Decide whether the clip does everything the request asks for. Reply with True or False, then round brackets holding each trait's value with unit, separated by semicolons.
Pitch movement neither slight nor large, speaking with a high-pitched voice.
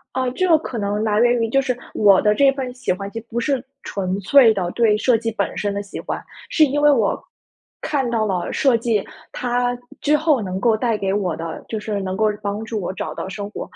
True (3.7 semitones; 225 Hz)